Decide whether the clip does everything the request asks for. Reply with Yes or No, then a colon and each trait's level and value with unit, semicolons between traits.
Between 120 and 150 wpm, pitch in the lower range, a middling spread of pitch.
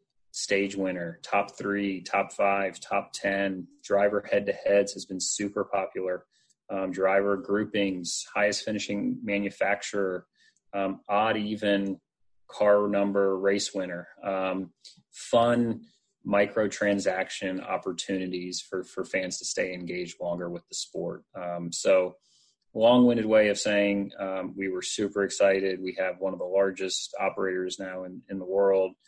No: average, 140 wpm; low, 100 Hz; narrow, 1.3 semitones